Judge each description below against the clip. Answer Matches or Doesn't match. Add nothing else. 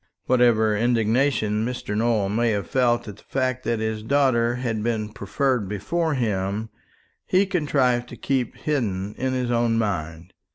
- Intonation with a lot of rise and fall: Doesn't match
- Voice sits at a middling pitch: Doesn't match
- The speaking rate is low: Doesn't match